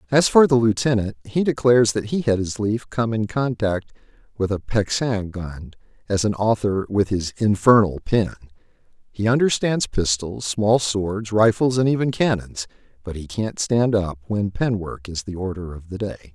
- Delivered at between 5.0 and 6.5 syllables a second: No, 4.7 syllables/s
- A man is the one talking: Yes, male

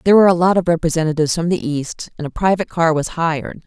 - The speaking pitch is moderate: Yes, medium, 165 Hz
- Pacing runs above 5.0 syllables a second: Yes, 7.2 syllables/s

